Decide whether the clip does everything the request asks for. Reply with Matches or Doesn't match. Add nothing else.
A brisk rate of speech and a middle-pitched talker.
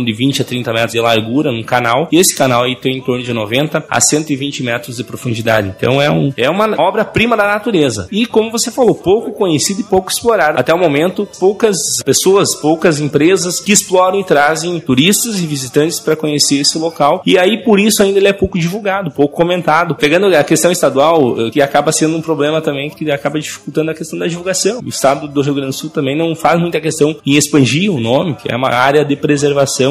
Matches